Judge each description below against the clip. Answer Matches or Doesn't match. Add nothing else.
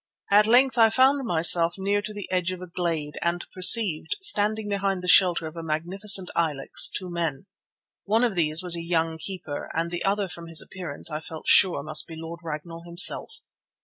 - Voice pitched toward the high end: Doesn't match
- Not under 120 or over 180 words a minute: Doesn't match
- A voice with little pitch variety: Doesn't match